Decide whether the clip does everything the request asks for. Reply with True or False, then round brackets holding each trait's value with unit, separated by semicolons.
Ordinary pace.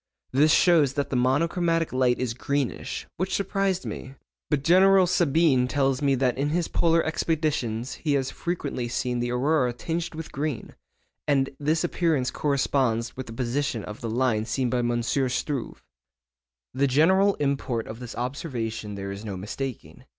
True (160 wpm)